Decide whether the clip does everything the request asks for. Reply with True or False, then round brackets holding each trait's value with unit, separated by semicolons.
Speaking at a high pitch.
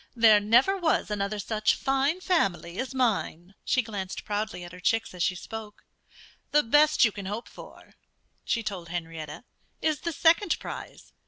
True (215 Hz)